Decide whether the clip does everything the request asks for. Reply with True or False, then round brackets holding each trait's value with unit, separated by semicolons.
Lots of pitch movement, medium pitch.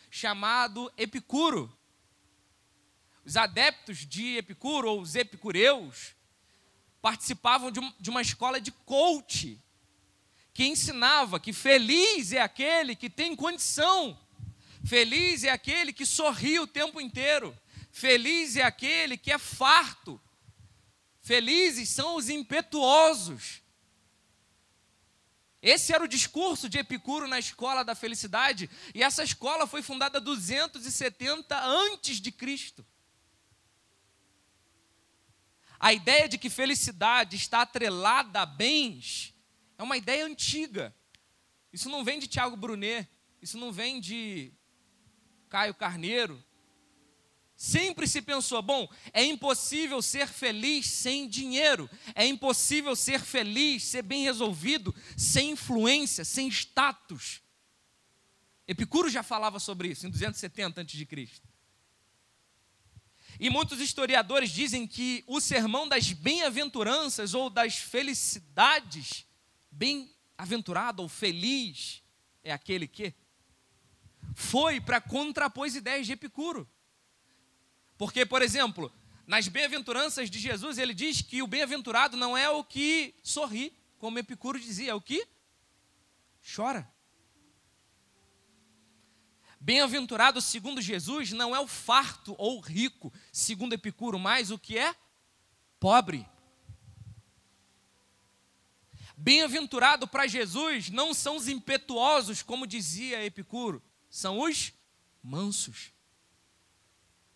False (6.6 semitones; 245 Hz)